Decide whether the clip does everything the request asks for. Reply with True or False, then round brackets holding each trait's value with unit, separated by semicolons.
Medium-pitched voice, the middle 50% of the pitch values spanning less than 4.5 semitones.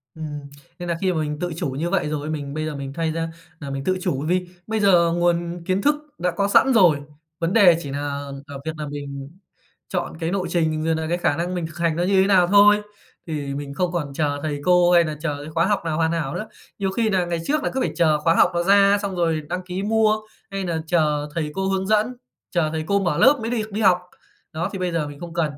True (170 Hz; 3.6 semitones)